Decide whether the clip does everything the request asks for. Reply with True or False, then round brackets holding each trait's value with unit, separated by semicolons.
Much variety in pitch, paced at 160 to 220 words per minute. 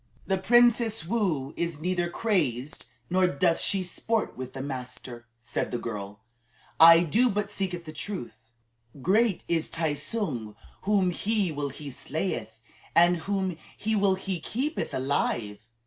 False (6.6 semitones; 145 wpm)